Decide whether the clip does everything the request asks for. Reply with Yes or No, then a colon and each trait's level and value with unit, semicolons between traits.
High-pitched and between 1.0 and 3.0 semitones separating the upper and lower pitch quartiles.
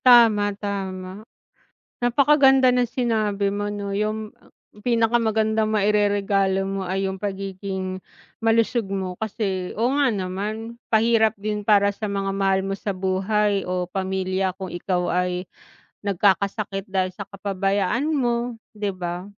Yes: high, 200 Hz; narrow, 2.4 semitones